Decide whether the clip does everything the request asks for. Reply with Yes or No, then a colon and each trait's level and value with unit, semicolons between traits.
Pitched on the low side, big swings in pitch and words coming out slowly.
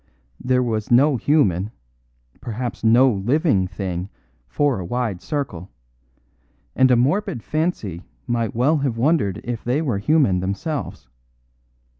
Yes: low, 120 Hz; wide, 6.1 semitones; slow, 125 wpm